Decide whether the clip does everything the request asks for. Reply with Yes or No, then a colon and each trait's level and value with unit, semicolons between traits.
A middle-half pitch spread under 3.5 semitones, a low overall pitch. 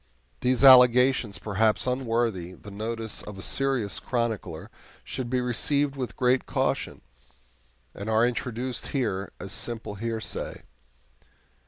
Yes: average, 3.1 semitones; low, 115 Hz